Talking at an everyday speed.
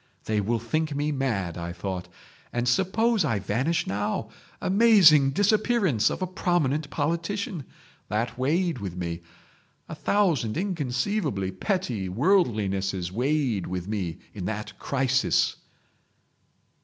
No: slow, 115 wpm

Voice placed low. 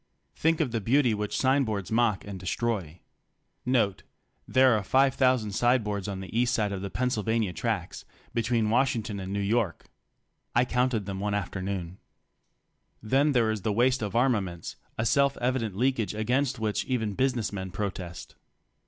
Yes: low, 110 Hz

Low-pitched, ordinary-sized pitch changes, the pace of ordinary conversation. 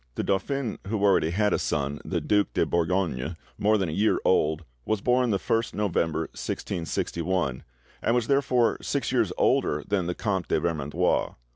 Yes: very low, 95 Hz; average, 4.7 semitones; average, 170 wpm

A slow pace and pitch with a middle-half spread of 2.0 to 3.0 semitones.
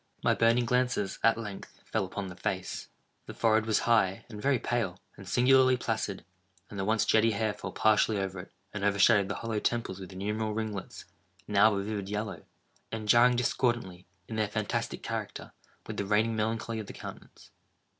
No: average, 185 wpm; narrow, 2.4 semitones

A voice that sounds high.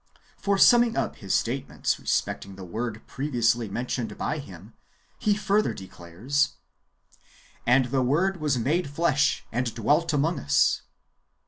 No: low, 130 Hz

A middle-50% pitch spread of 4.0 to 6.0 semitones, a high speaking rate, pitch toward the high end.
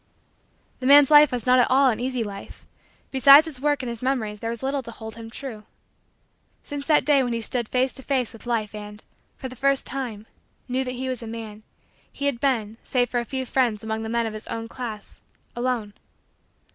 No: average, 3.1 semitones; fast, 220 wpm; high, 245 Hz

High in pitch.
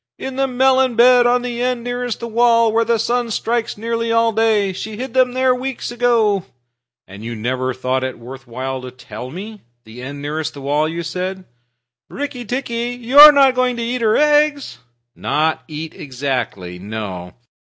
Yes: high, 225 Hz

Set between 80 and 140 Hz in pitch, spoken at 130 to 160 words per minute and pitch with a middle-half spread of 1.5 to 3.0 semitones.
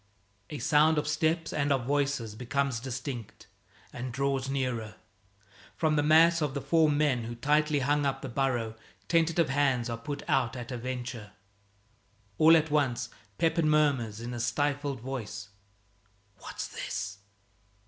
No: low, 135 Hz; average, 150 wpm; average, 3.7 semitones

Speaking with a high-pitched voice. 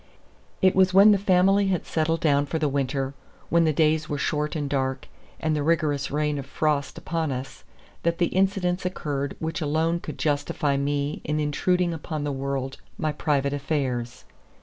No: medium, 150 Hz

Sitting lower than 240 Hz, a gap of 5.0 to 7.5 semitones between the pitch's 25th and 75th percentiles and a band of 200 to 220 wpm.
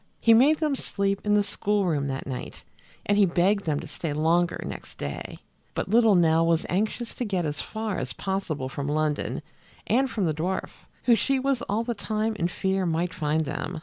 Yes: high, 190 Hz; wide, 5.4 semitones; fast, 205 wpm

